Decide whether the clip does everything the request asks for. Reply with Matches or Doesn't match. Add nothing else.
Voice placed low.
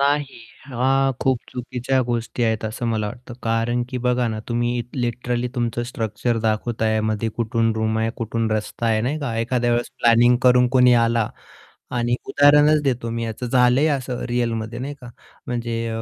Matches